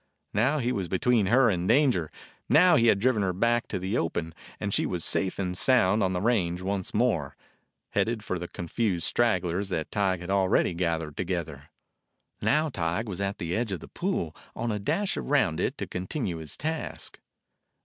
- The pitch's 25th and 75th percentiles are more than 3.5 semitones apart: Yes, average, 5.1 semitones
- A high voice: No, very low, 95 Hz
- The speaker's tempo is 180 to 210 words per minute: Yes, average, 190 wpm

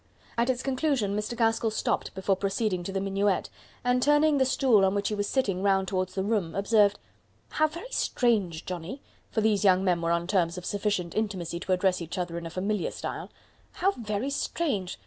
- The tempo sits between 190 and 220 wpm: Yes, average, 200 wpm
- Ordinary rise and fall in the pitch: Yes, average, 4.1 semitones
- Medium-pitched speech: No, high, 200 Hz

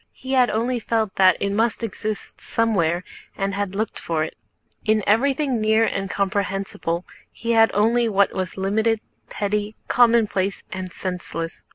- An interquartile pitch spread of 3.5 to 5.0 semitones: No, average, 2.8 semitones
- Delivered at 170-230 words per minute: No, average, 155 wpm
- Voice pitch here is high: Yes, high, 210 Hz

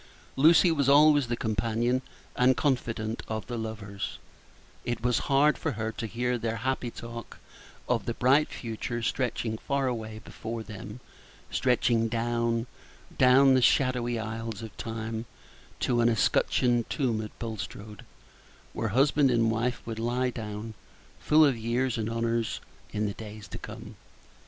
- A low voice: Yes, low, 115 Hz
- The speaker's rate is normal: Yes, average, 145 wpm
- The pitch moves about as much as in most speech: No, narrow, 2.2 semitones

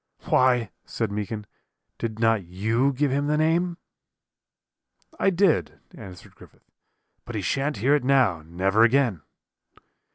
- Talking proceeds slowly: Yes, slow, 130 wpm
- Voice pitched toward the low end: Yes, low, 120 Hz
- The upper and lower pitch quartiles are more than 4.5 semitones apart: Yes, wide, 5.4 semitones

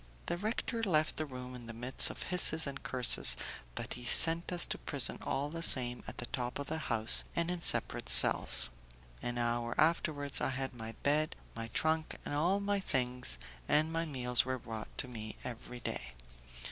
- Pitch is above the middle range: No, low, 135 Hz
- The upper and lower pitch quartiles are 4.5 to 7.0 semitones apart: Yes, average, 4.8 semitones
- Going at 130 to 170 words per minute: No, average, 190 wpm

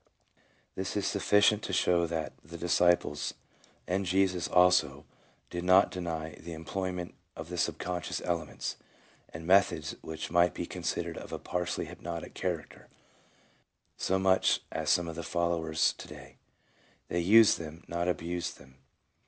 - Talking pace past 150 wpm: No, average, 145 wpm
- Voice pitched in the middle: No, very low, 85 Hz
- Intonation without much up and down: Yes, narrow, 2.0 semitones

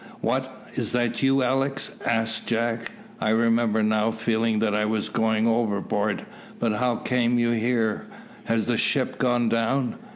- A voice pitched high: No, low, 115 Hz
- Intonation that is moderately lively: No, narrow, 1.6 semitones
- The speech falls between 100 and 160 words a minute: Yes, average, 155 wpm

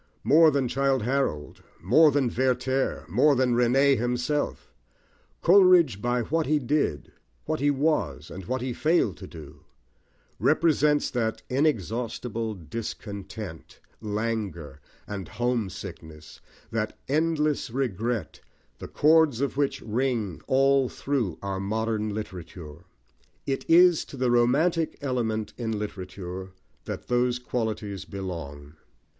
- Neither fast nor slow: No, slow, 115 wpm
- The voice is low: Yes, low, 120 Hz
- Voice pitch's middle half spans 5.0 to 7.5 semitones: Yes, wide, 5.6 semitones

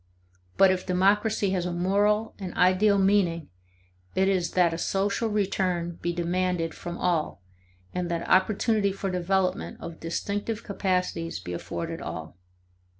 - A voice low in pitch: No, medium, 185 Hz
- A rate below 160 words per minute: Yes, average, 140 wpm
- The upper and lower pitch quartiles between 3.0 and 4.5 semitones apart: No, narrow, 2.5 semitones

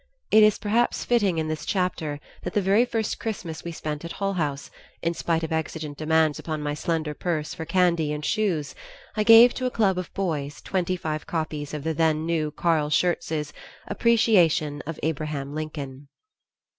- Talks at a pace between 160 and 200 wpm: Yes, average, 180 wpm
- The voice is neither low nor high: Yes, medium, 160 Hz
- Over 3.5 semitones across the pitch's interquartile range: Yes, average, 3.9 semitones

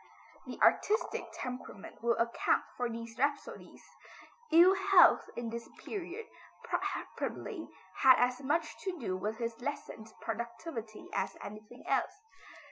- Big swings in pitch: Yes, wide, 6.5 semitones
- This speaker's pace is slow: Yes, slow, 125 wpm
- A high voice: Yes, high, 245 Hz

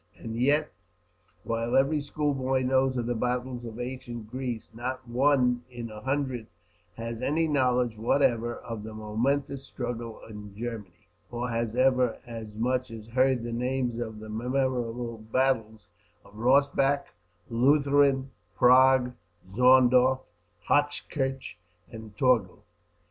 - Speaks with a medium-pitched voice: No, low, 125 Hz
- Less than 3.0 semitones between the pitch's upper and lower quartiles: Yes, narrow, 2.5 semitones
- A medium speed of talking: No, slow, 125 wpm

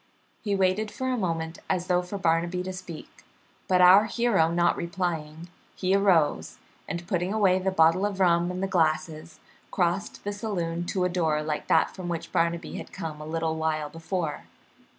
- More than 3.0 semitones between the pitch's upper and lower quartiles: No, narrow, 2.6 semitones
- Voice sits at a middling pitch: Yes, medium, 175 Hz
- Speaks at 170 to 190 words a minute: Yes, average, 180 wpm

